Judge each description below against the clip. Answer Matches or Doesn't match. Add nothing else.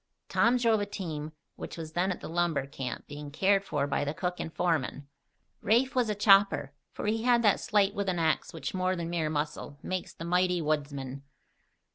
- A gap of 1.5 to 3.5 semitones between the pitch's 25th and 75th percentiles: Doesn't match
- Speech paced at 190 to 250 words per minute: Matches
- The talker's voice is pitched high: Doesn't match